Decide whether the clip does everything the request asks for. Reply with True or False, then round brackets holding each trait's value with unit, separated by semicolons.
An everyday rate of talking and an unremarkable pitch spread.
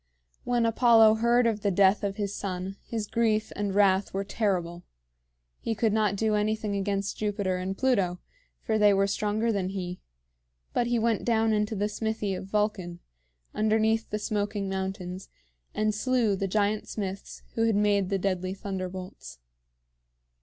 False (160 wpm; 2.2 semitones)